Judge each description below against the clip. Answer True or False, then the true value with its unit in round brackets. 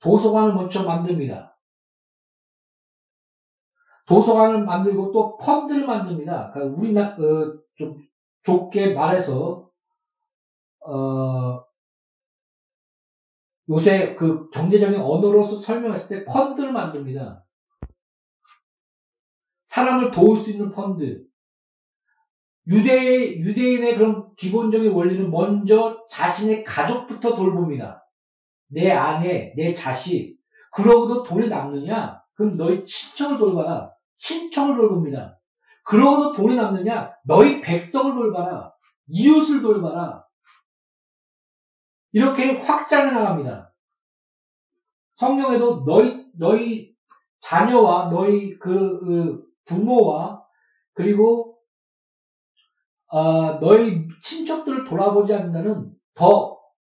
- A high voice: True (210 Hz)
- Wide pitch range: True (5.9 semitones)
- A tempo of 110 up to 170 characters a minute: False (215 characters per minute)